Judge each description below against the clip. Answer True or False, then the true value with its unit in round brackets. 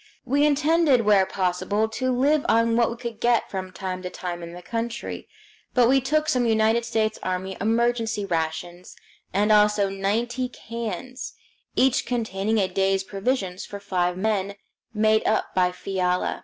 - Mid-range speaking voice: False (215 Hz)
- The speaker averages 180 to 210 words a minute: False (155 wpm)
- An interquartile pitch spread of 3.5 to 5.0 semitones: True (4.0 semitones)